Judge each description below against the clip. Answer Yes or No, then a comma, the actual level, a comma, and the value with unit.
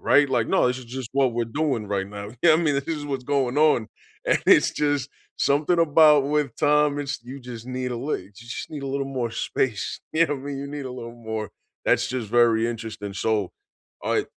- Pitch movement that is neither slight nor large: Yes, average, 3.8 semitones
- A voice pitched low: Yes, low, 130 Hz